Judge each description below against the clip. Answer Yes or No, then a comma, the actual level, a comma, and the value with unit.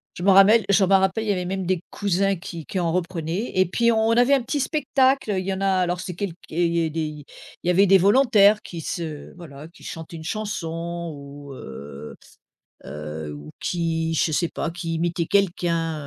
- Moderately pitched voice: Yes, medium, 175 Hz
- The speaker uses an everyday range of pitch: Yes, average, 3.4 semitones